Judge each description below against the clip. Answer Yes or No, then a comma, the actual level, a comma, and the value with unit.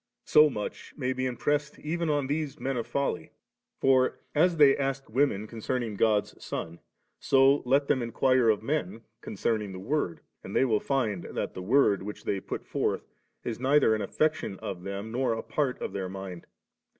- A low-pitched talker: Yes, low, 130 Hz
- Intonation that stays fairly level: No, average, 5.1 semitones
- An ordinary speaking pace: Yes, average, 180 wpm